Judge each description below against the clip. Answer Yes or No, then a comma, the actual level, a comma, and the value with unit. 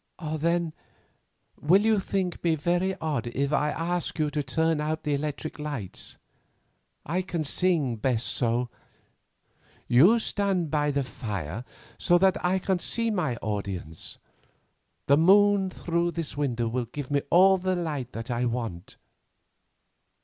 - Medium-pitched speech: Yes, medium, 150 Hz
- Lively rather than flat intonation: Yes, wide, 6.0 semitones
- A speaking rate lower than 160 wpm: Yes, average, 140 wpm